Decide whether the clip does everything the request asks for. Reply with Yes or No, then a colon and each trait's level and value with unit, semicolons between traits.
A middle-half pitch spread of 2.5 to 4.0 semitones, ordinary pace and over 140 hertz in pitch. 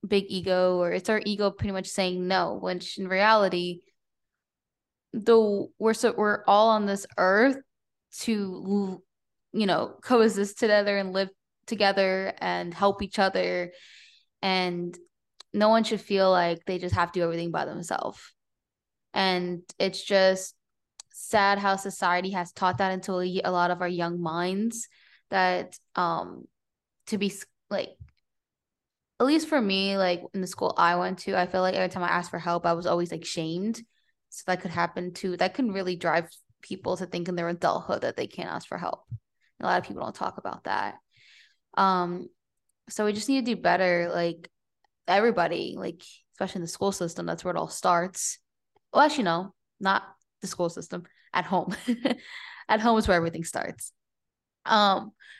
Yes: average, 2.9 semitones; average, 175 wpm; high, 190 Hz